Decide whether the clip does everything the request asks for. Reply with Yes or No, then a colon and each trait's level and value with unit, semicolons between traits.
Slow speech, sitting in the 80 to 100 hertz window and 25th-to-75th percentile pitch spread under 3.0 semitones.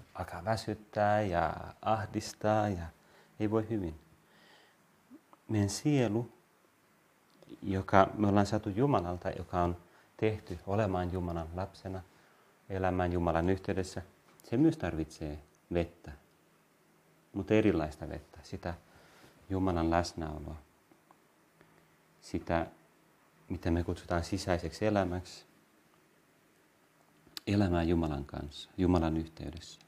No: slow, 90 wpm; very low, 90 Hz; average, 3.6 semitones